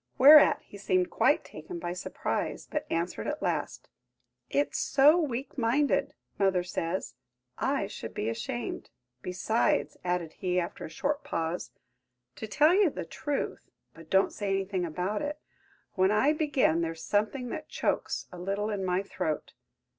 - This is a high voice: Yes, high, 195 Hz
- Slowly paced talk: No, average, 145 wpm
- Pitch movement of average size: No, wide, 7.9 semitones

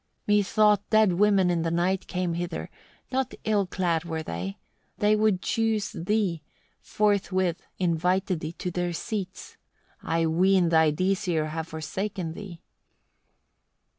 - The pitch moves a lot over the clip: No, average, 3.6 semitones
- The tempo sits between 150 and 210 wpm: No, slow, 135 wpm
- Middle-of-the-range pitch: Yes, medium, 180 Hz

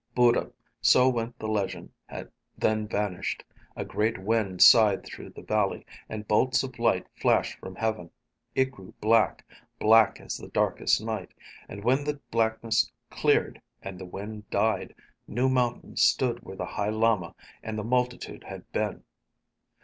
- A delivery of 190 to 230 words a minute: No, average, 150 wpm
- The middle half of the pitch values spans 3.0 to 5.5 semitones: No, narrow, 2.6 semitones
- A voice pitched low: Yes, low, 110 Hz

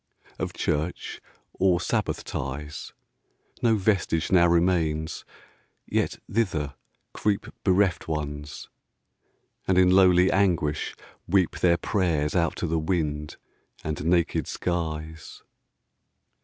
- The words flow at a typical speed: No, slow, 105 wpm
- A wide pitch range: No, average, 3.3 semitones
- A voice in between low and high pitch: No, very low, 85 Hz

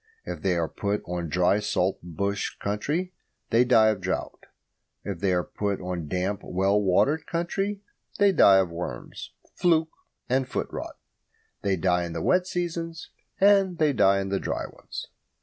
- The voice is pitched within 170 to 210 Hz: No, low, 100 Hz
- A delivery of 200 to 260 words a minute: No, average, 165 wpm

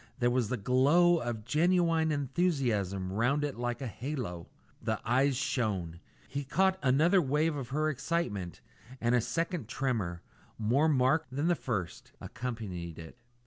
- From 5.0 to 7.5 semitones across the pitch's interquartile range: Yes, wide, 5.6 semitones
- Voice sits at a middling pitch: No, low, 130 Hz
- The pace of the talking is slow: No, average, 145 wpm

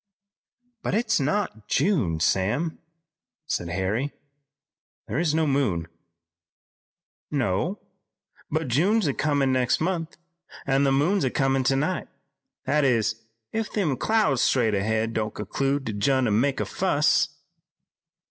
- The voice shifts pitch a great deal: Yes, wide, 6.1 semitones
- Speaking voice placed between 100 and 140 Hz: Yes, low, 135 Hz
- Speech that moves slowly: Yes, slow, 125 wpm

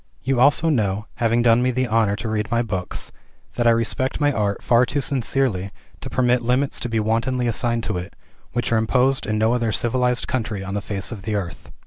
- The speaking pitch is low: Yes, low, 115 Hz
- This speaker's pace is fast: Yes, fast, 215 wpm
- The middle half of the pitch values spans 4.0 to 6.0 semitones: No, average, 2.7 semitones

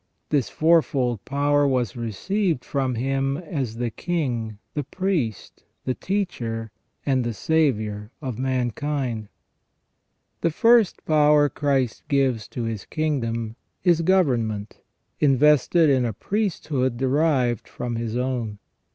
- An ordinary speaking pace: No, slow, 115 wpm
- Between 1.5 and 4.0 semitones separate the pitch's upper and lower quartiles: No, average, 4.5 semitones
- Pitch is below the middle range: Yes, low, 130 Hz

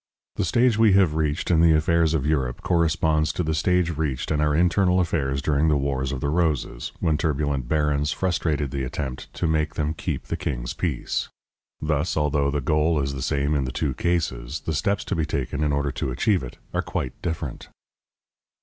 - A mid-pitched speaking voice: No, very low, 75 Hz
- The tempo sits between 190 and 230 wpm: Yes, average, 200 wpm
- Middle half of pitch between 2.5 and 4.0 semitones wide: Yes, average, 2.8 semitones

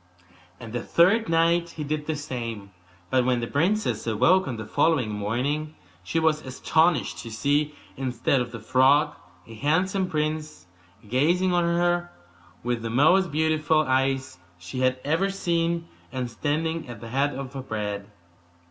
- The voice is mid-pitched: Yes, medium, 145 Hz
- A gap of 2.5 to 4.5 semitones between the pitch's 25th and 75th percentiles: No, average, 5.2 semitones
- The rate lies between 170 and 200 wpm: No, average, 155 wpm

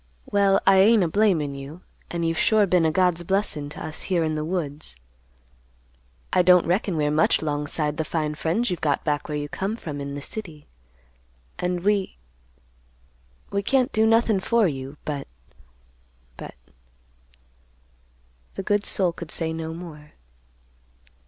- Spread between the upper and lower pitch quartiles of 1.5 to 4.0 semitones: No, average, 4.8 semitones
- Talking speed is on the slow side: No, average, 150 wpm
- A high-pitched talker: No, medium, 160 Hz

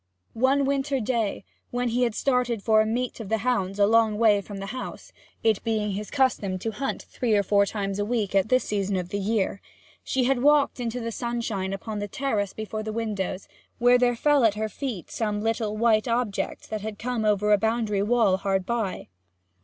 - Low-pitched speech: No, high, 220 Hz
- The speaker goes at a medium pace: No, fast, 210 wpm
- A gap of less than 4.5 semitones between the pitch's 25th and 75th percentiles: Yes, average, 3.1 semitones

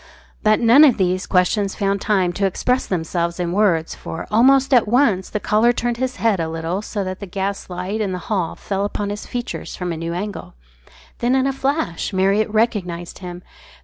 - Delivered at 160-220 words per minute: Yes, average, 200 wpm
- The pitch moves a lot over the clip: No, average, 4.1 semitones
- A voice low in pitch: No, high, 200 Hz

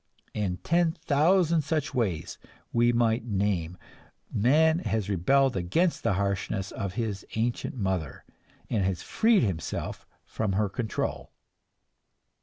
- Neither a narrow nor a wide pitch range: No, wide, 6.4 semitones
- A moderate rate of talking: No, slow, 120 wpm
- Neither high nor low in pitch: No, low, 110 Hz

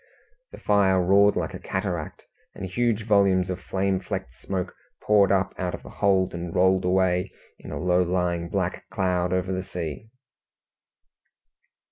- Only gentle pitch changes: Yes, narrow, 1.5 semitones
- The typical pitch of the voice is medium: No, very low, 95 Hz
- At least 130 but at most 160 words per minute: Yes, average, 155 wpm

